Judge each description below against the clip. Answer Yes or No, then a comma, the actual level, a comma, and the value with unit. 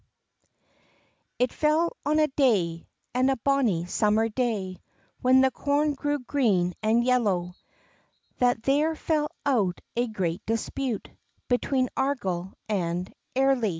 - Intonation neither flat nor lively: No, wide, 5.7 semitones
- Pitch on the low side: No, high, 245 Hz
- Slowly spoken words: Yes, slow, 120 wpm